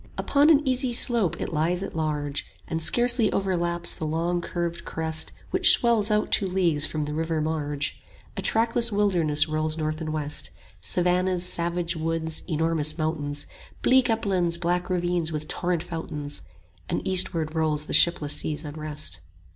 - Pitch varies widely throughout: No, average, 2.9 semitones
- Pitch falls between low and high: Yes, medium, 165 Hz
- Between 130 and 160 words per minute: Yes, average, 155 wpm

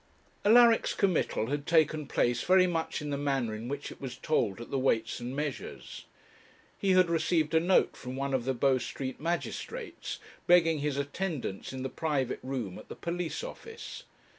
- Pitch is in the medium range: Yes, medium, 145 Hz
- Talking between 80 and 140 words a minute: No, average, 180 wpm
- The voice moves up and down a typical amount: Yes, average, 4.7 semitones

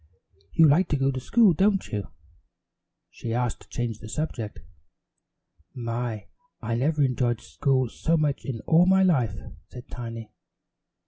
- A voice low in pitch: Yes, low, 130 Hz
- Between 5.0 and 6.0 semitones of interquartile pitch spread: Yes, average, 5.3 semitones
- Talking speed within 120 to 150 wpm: Yes, average, 145 wpm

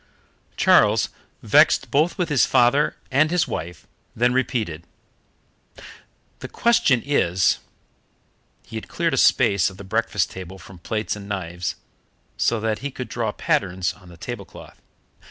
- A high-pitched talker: No, low, 105 Hz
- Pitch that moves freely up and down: Yes, wide, 5.7 semitones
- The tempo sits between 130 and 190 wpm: Yes, average, 145 wpm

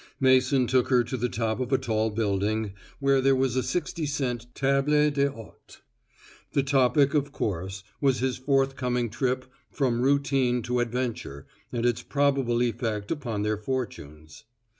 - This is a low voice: Yes, low, 125 Hz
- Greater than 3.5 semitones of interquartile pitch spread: No, average, 3.2 semitones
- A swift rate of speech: No, average, 150 wpm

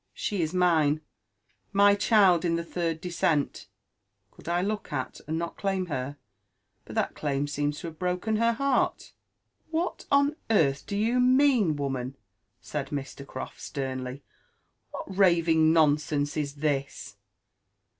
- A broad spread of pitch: Yes, wide, 5.7 semitones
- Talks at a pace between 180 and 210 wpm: No, average, 145 wpm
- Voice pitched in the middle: Yes, medium, 165 Hz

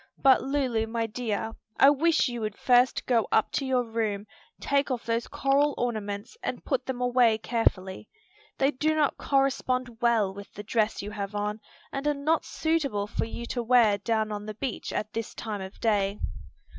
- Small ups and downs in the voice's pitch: No, average, 4.0 semitones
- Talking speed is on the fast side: No, average, 185 wpm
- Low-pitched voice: No, high, 230 Hz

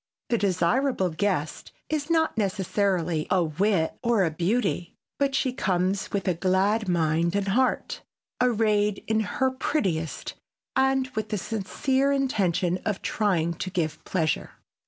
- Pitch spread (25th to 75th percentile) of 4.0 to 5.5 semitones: Yes, average, 5.2 semitones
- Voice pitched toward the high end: Yes, high, 200 Hz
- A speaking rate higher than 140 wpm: No, slow, 135 wpm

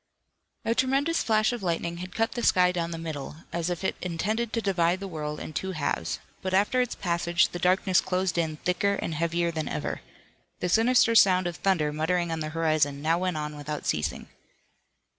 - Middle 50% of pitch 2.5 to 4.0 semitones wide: Yes, average, 3.2 semitones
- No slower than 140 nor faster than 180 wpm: No, average, 200 wpm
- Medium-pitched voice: Yes, medium, 175 Hz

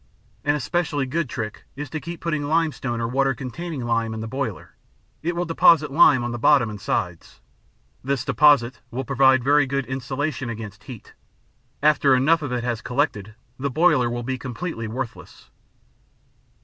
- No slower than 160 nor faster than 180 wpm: Yes, average, 165 wpm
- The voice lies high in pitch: No, low, 130 Hz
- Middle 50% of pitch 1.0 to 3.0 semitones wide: No, average, 3.7 semitones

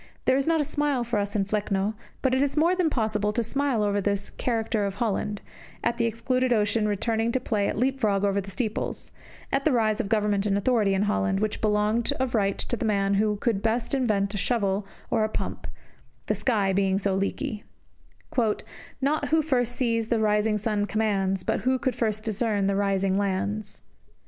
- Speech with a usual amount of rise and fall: Yes, average, 3.1 semitones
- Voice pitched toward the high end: Yes, high, 215 Hz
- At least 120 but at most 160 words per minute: No, average, 200 wpm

